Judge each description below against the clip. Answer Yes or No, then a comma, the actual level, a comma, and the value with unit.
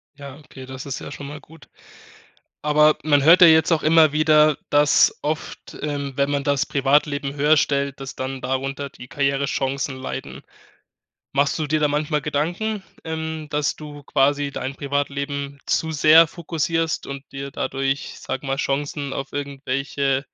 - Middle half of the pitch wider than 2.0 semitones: No, narrow, 1.7 semitones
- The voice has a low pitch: No, medium, 145 Hz